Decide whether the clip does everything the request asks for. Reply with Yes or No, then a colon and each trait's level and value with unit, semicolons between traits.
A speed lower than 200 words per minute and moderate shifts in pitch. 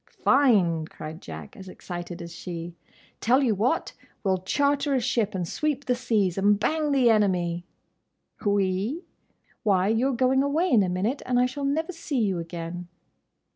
No: average, 165 wpm; wide, 6.9 semitones